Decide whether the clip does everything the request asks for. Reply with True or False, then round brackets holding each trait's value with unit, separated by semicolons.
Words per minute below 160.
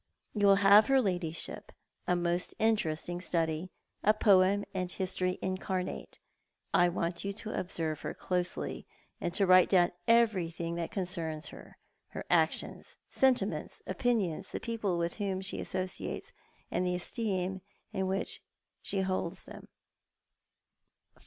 True (140 wpm)